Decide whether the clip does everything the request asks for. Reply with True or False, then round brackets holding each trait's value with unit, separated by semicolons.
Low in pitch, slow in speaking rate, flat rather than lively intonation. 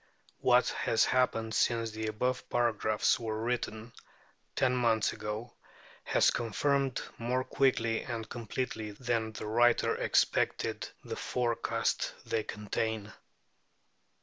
True (115 Hz; 110 wpm; 2.0 semitones)